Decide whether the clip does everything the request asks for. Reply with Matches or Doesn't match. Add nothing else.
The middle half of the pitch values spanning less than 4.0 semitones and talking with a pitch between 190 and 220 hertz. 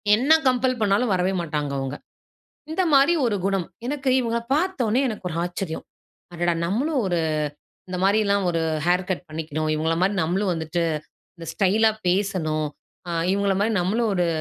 Doesn't match